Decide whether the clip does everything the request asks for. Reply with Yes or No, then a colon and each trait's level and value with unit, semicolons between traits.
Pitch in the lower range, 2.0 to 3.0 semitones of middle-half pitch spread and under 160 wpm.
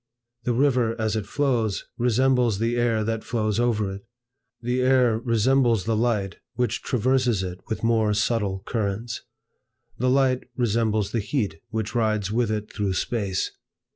Yes: low, 115 Hz; narrow, 2.6 semitones; average, 150 wpm